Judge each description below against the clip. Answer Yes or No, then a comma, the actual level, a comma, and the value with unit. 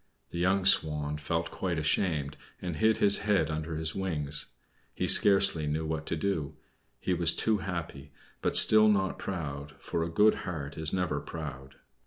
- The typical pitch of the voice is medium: No, very low, 80 Hz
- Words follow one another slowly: No, average, 170 wpm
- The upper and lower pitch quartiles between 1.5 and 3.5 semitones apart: No, average, 4.0 semitones